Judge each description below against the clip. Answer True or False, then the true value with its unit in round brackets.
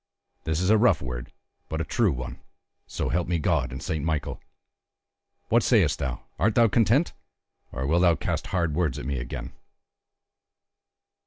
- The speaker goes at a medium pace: True (160 wpm)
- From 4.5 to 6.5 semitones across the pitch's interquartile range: True (5.3 semitones)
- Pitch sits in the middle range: False (80 Hz)